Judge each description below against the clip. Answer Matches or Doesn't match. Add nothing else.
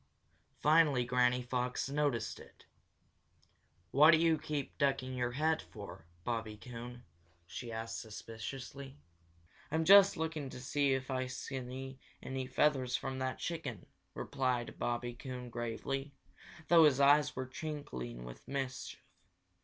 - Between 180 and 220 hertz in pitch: Doesn't match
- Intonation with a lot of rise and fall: Doesn't match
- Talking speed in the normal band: Doesn't match